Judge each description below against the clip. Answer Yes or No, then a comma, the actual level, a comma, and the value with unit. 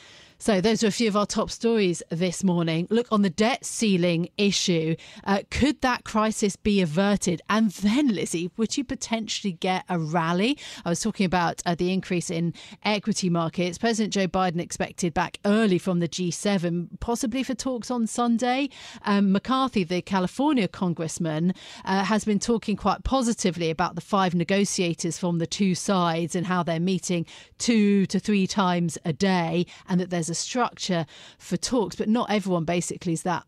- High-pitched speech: Yes, high, 195 Hz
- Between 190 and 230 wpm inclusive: No, average, 175 wpm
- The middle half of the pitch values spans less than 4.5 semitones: Yes, average, 3.7 semitones